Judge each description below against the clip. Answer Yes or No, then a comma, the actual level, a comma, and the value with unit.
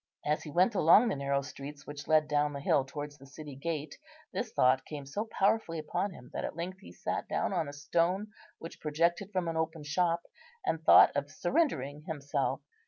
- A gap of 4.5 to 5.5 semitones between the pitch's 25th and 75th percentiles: No, average, 3.3 semitones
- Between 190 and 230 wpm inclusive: Yes, average, 200 wpm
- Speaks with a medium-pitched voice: Yes, medium, 155 Hz